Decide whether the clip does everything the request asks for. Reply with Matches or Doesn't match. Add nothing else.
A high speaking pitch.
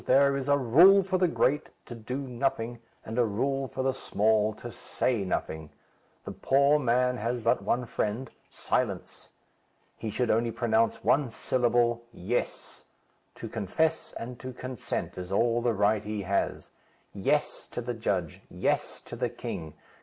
Doesn't match